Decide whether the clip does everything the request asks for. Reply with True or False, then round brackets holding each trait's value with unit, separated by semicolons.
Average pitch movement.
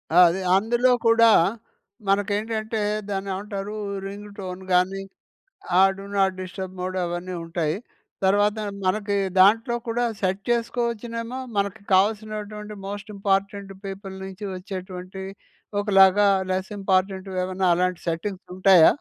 False (2.0 semitones)